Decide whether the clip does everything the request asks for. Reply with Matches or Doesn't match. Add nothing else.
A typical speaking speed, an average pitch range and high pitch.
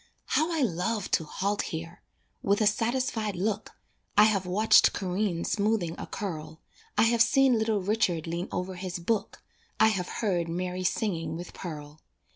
Matches